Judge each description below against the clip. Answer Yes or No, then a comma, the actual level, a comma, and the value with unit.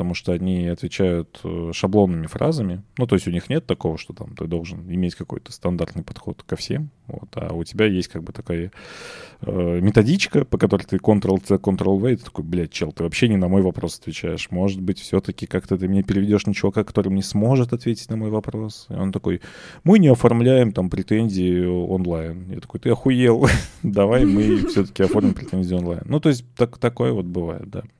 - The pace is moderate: No, fast, 195 wpm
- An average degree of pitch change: Yes, average, 4.4 semitones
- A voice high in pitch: No, low, 100 Hz